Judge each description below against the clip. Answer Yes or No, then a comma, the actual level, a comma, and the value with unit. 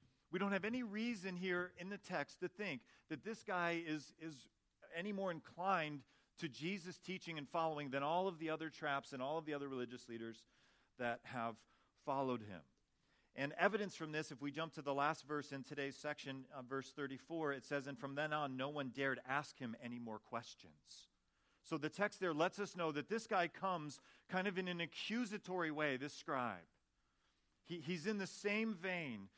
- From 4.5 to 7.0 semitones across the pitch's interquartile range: Yes, average, 4.9 semitones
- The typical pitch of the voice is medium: Yes, medium, 155 Hz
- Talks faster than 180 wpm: Yes, average, 200 wpm